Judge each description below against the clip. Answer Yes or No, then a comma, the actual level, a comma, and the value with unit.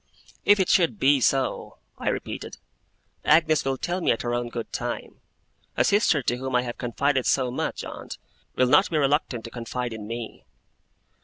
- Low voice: Yes, low, 130 Hz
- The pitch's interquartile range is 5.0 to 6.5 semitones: No, average, 3.8 semitones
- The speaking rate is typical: Yes, average, 180 wpm